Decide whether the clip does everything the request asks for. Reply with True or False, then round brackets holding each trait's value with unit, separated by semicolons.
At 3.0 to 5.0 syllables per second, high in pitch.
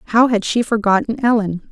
True (4.8 syllables/s; 220 Hz)